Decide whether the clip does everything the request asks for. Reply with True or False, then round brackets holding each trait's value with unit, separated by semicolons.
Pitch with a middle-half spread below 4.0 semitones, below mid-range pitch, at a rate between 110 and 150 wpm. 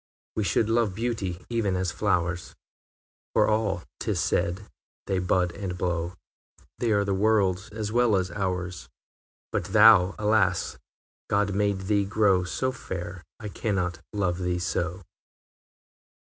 True (2.9 semitones; 95 Hz; 140 wpm)